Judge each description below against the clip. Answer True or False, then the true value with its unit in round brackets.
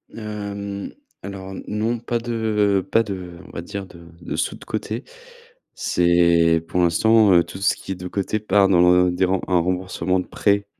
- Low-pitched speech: True (95 Hz)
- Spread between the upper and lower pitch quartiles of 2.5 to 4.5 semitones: True (2.8 semitones)